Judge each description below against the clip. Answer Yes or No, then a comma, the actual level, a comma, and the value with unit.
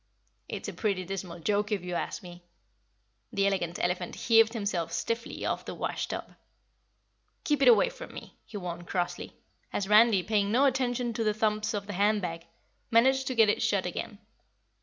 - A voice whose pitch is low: No, high, 205 Hz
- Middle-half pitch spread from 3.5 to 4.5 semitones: Yes, average, 4.1 semitones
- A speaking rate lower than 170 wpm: No, average, 180 wpm